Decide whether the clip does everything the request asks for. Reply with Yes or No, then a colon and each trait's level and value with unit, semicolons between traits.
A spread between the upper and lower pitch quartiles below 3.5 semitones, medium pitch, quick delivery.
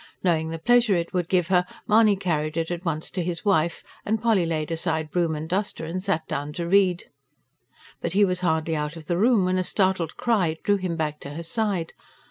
Yes: average, 3.1 semitones; medium, 175 Hz; fast, 220 wpm